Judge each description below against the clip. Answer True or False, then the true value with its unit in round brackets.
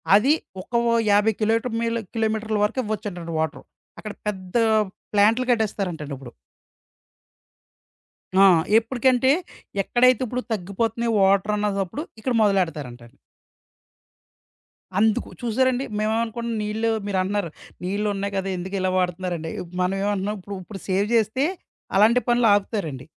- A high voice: True (210 Hz)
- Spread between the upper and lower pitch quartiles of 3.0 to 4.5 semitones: True (3.3 semitones)